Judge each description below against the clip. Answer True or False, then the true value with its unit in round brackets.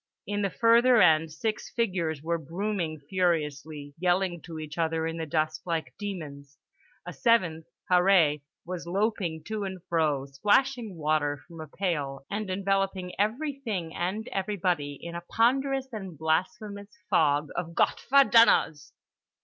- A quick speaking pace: False (140 wpm)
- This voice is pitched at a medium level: True (175 Hz)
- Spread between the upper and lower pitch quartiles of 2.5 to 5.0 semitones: True (4.5 semitones)